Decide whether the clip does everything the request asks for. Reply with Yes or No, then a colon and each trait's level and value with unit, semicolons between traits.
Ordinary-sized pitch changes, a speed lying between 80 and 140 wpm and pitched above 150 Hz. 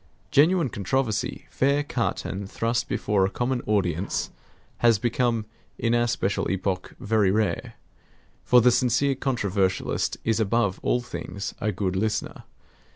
No: average, 3.7 semitones; slow, 135 wpm; low, 110 Hz